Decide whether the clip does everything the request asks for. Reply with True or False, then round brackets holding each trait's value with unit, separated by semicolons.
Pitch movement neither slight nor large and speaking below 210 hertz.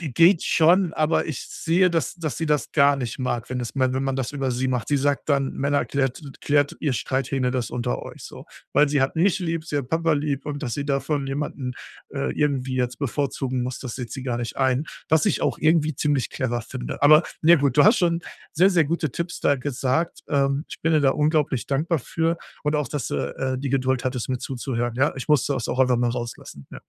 True (3.1 semitones; 140 Hz)